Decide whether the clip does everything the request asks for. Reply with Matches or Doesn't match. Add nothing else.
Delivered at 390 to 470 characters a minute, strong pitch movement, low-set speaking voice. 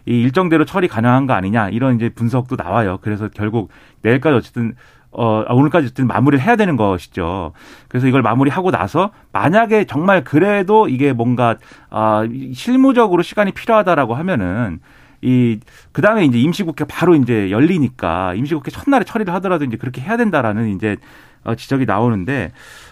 Matches